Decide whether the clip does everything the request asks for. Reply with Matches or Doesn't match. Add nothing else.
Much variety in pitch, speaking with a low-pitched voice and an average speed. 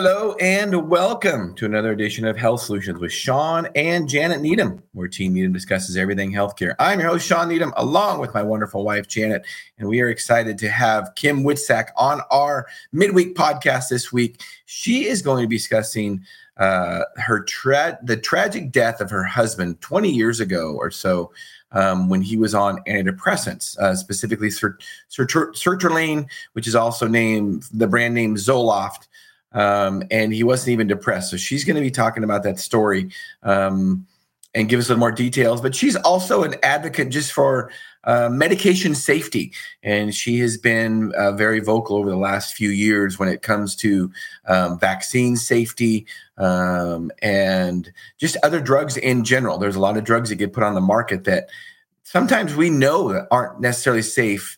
Matches